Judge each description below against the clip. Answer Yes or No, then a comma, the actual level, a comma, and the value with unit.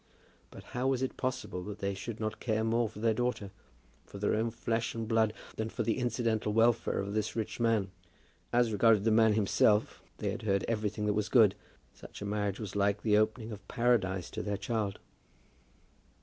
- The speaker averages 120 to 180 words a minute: No, average, 195 wpm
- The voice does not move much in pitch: Yes, narrow, 2.0 semitones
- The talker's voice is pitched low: Yes, low, 110 Hz